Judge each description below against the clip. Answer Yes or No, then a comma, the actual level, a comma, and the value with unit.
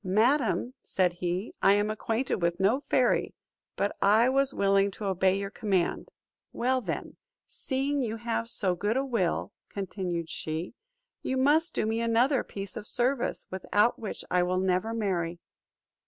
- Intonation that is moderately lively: Yes, average, 4.6 semitones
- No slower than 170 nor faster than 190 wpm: No, average, 155 wpm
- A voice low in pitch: No, high, 210 Hz